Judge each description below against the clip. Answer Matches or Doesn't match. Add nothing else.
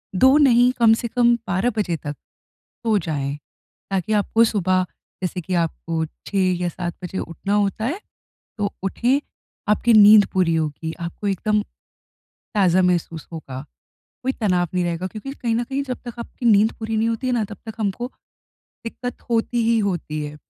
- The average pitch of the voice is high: Matches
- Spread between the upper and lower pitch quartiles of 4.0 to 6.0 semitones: Matches